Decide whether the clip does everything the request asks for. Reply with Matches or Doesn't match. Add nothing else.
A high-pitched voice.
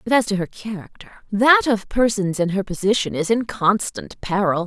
Matches